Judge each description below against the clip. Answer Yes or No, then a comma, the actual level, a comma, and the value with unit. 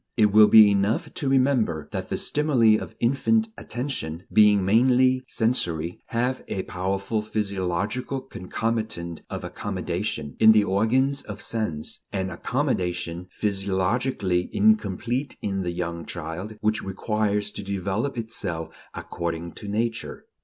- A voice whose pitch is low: Yes, low, 105 Hz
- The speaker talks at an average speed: No, slow, 125 wpm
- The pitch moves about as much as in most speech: Yes, average, 4.5 semitones